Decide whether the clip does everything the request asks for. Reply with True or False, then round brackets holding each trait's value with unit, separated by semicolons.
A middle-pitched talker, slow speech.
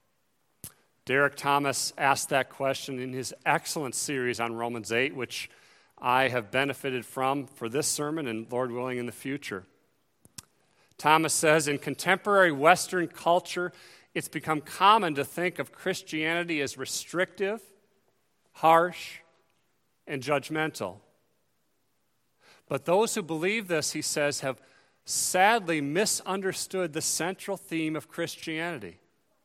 True (155 Hz; 120 wpm)